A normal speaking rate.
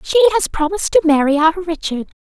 Yes: average, 190 wpm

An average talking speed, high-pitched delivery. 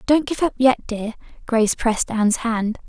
Yes: average, 190 wpm; high, 235 Hz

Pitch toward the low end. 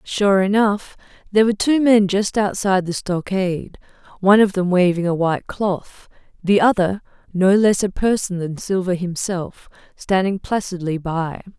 No: high, 190 Hz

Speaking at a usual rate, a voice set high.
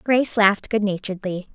Yes: average, 155 wpm; high, 205 Hz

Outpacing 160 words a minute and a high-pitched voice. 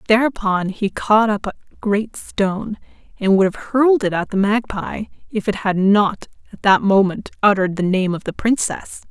Yes: average, 185 wpm; high, 205 Hz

